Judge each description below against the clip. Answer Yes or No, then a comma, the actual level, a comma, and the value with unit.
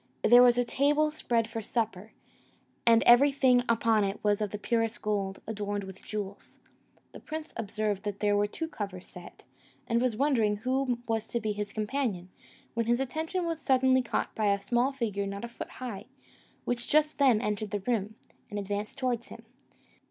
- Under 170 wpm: No, average, 180 wpm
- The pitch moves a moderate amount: Yes, average, 3.6 semitones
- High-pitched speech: Yes, high, 225 Hz